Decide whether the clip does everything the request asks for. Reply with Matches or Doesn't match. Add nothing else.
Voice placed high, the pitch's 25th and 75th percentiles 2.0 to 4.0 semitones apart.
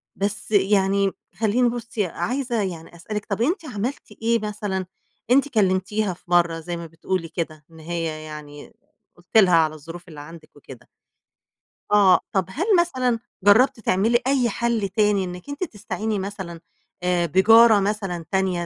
Doesn't match